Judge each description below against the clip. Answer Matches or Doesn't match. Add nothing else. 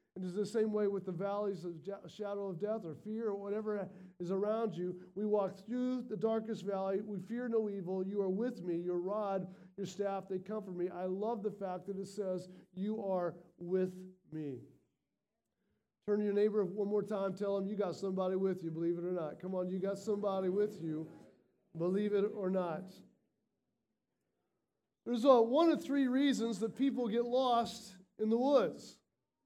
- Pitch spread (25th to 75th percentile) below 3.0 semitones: Matches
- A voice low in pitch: Doesn't match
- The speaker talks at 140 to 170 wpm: Doesn't match